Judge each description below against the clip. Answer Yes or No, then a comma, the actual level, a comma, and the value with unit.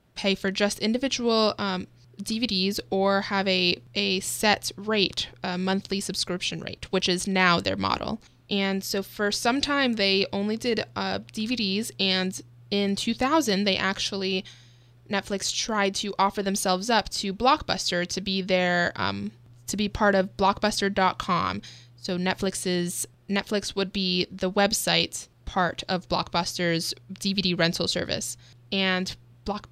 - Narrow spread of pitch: Yes, narrow, 2.2 semitones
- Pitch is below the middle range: No, high, 195 Hz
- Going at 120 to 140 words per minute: Yes, slow, 135 wpm